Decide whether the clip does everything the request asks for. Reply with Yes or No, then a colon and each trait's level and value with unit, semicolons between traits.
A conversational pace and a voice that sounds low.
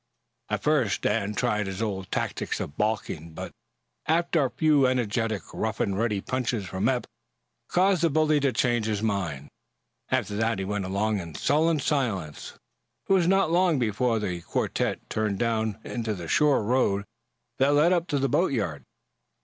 Yes: average, 165 wpm; low, 115 Hz